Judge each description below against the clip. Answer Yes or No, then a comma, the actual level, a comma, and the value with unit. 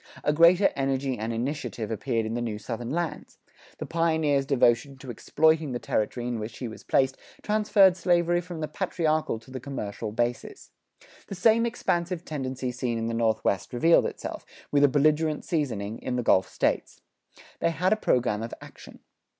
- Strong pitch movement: Yes, wide, 5.9 semitones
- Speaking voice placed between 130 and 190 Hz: Yes, low, 135 Hz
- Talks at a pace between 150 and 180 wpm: Yes, average, 175 wpm